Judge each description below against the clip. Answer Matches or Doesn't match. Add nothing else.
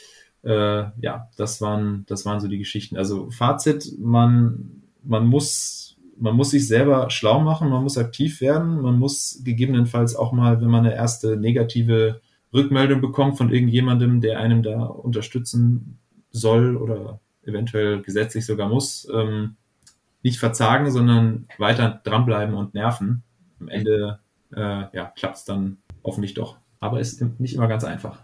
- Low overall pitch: Matches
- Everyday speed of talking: Matches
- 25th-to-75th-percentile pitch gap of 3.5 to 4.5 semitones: Doesn't match